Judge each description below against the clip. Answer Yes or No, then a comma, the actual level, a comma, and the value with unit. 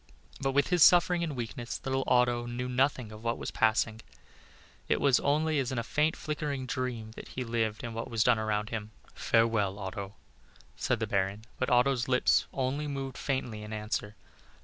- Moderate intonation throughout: Yes, average, 3.6 semitones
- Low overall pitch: Yes, low, 120 Hz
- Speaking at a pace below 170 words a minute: No, average, 185 wpm